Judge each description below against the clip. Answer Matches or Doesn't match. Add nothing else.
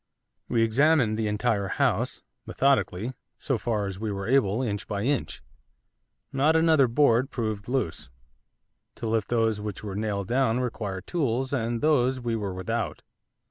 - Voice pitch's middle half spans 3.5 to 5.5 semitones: Matches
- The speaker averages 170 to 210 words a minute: Doesn't match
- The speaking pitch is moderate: Doesn't match